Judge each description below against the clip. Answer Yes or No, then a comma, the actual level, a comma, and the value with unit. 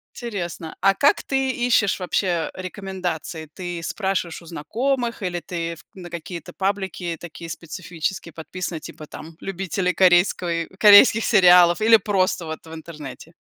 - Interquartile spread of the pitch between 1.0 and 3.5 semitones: Yes, average, 2.8 semitones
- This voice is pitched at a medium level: Yes, medium, 180 Hz